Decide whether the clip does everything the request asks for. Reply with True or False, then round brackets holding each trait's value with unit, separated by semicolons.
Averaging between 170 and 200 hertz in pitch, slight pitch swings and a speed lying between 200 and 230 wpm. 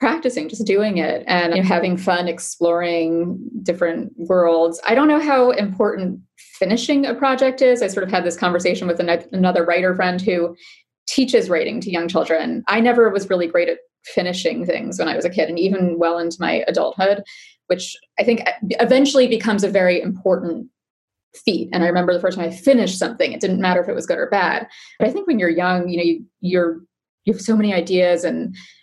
False (185 Hz; 5.4 semitones; 205 wpm)